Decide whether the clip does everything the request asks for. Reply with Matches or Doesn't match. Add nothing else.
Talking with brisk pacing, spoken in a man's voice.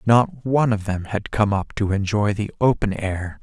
Matches